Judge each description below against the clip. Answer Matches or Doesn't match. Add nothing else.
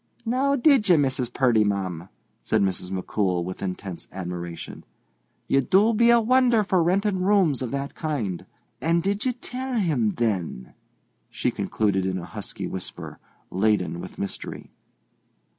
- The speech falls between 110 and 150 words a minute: Matches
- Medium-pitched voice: Doesn't match